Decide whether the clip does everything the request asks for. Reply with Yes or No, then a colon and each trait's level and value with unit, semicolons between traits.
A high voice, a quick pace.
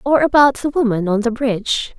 Yes: high, 245 Hz; fast, 210 wpm